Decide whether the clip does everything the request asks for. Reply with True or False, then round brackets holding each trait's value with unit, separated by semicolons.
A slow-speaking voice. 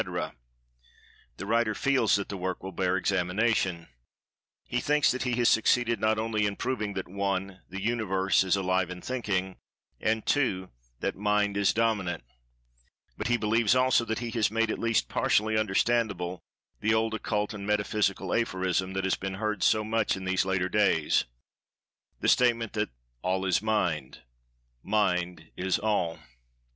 False (155 wpm)